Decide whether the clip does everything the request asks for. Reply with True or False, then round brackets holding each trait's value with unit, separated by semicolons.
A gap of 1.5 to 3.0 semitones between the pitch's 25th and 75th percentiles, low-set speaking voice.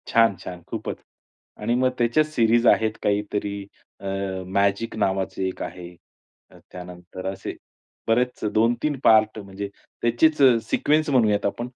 False (3.4 semitones; 110 Hz)